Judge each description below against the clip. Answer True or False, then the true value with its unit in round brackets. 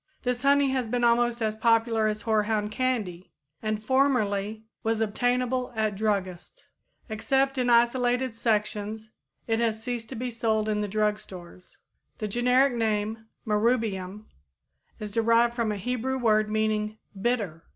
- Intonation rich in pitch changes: False (2.4 semitones)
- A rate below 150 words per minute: True (140 wpm)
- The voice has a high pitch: True (225 Hz)